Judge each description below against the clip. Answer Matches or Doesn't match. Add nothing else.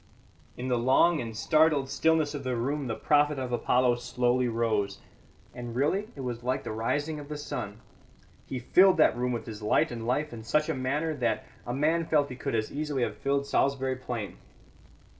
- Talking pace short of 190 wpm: Doesn't match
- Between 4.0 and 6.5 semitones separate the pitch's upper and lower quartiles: Doesn't match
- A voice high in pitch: Doesn't match